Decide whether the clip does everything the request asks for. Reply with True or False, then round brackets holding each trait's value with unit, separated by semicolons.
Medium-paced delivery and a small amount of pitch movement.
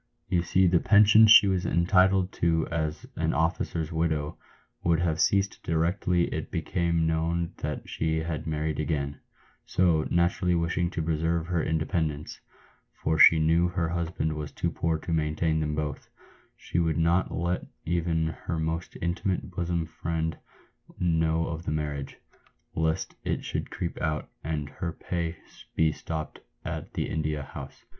True (160 wpm; 1.7 semitones)